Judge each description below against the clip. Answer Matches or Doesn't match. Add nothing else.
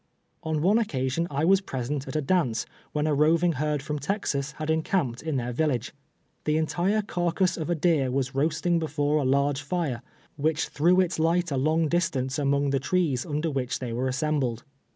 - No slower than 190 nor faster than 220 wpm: Matches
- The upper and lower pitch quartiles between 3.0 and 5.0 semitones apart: Matches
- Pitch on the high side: Doesn't match